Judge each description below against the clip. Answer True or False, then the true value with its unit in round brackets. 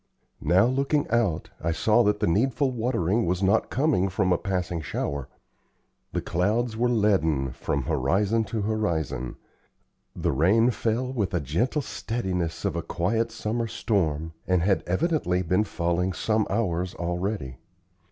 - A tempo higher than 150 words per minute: False (145 wpm)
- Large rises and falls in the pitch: False (5.0 semitones)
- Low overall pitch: True (100 Hz)